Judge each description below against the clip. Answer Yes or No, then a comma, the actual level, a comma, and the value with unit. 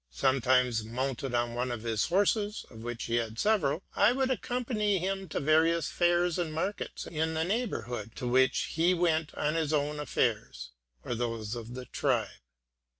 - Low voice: No, medium, 150 Hz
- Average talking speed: Yes, average, 170 wpm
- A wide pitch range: Yes, wide, 6.8 semitones